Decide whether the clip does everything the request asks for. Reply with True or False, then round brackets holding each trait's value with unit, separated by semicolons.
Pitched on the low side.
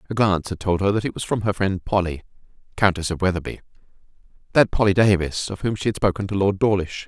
True (95 Hz)